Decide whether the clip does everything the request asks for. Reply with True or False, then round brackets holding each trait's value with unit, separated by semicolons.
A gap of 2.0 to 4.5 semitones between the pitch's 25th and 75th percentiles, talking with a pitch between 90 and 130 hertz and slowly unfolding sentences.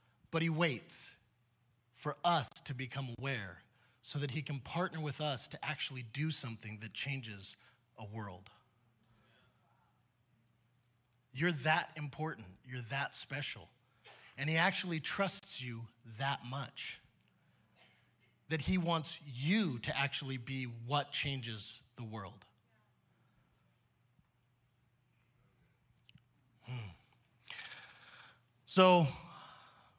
True (4.1 semitones; 125 Hz; 100 wpm)